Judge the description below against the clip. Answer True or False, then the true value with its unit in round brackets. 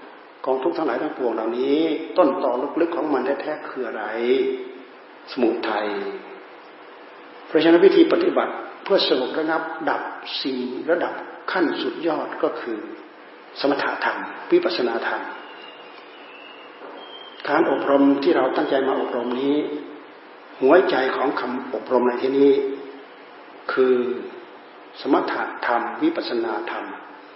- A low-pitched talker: False (340 Hz)